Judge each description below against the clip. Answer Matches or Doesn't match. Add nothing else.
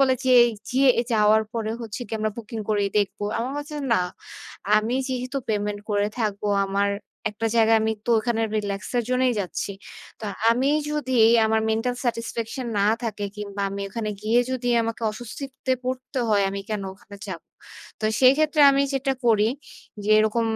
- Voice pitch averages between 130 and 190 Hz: Doesn't match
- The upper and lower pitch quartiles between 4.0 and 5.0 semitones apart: Doesn't match